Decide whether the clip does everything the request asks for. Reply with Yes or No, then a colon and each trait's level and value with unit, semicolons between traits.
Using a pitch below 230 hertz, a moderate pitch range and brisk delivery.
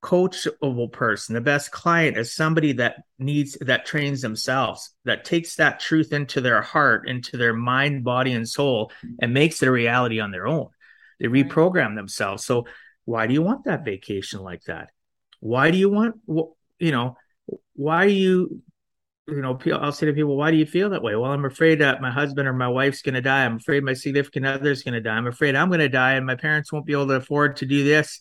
Yes: medium, 140 Hz; average, 3.6 semitones; fast, 215 wpm